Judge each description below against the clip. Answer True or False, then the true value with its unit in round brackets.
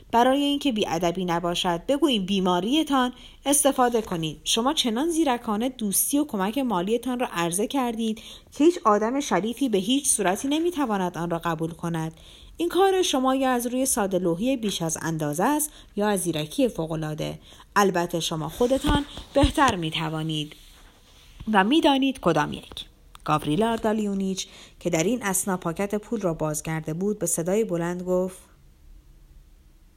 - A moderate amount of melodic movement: False (7.4 semitones)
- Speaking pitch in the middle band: False (195 Hz)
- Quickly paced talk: False (140 wpm)